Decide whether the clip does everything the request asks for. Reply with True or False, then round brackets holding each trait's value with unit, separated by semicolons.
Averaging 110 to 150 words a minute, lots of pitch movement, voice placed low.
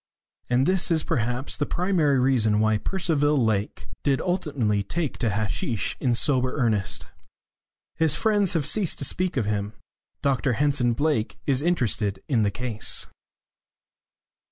True (140 wpm; 5.7 semitones; 130 Hz)